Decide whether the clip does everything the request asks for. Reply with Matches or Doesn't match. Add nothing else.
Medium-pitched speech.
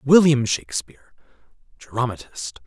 Doesn't match